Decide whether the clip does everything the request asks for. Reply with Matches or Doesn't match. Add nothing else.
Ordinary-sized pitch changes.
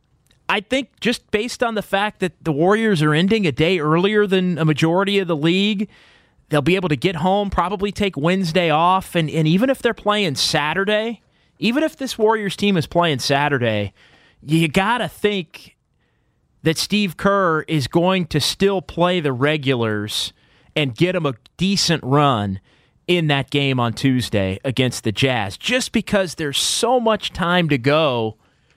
Doesn't match